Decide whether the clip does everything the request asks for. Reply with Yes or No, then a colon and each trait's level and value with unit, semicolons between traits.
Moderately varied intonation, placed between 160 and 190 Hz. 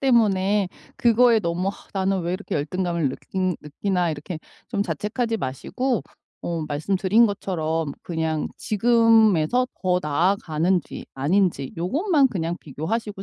Yes: average, 4.8 semitones; medium, 185 Hz